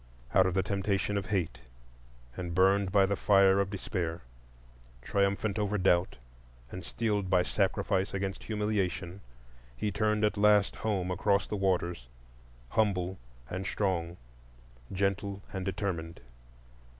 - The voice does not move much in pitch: Yes, narrow, 1.7 semitones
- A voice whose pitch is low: Yes, very low, 95 Hz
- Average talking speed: No, slow, 125 wpm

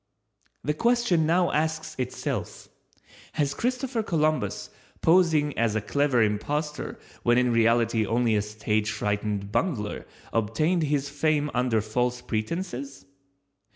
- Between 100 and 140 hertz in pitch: Yes, low, 135 Hz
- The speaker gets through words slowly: Yes, slow, 120 wpm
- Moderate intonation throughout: No, wide, 6.0 semitones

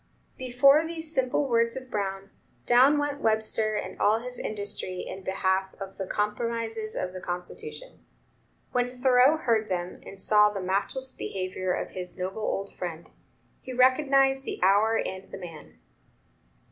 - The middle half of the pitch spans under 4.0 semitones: No, average, 5.1 semitones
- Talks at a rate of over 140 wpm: Yes, average, 150 wpm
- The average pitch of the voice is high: Yes, high, 220 Hz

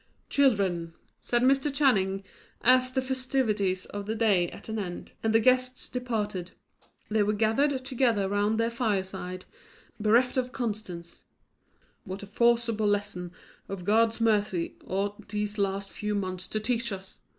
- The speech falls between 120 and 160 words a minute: Yes, average, 145 wpm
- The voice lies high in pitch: Yes, high, 215 Hz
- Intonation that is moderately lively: Yes, average, 3.5 semitones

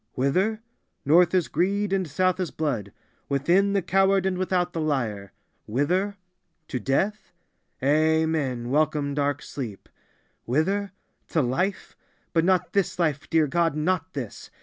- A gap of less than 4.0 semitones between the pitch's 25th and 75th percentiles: No, average, 4.7 semitones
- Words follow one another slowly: Yes, slow, 125 wpm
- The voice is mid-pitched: Yes, medium, 160 Hz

